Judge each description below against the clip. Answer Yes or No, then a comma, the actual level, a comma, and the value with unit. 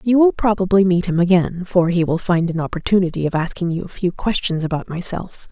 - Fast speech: Yes, fast, 220 wpm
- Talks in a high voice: No, medium, 180 Hz